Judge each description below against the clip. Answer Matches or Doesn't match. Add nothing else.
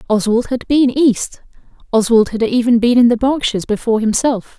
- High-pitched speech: Matches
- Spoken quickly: Doesn't match